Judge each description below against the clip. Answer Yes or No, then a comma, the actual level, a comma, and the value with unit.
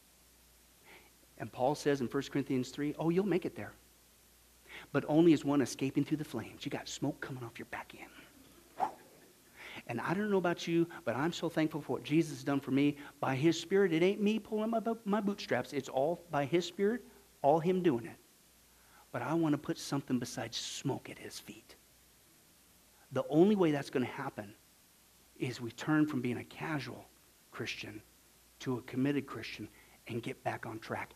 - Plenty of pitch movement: No, average, 4.7 semitones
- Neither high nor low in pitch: Yes, medium, 145 Hz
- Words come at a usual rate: Yes, average, 190 wpm